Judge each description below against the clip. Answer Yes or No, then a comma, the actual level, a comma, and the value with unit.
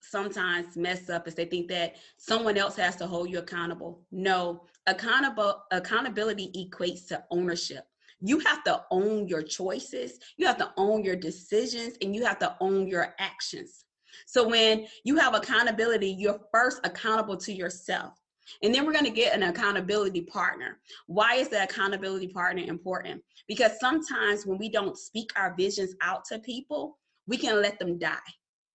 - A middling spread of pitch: Yes, average, 4.1 semitones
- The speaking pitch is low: No, high, 195 Hz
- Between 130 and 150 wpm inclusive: No, average, 165 wpm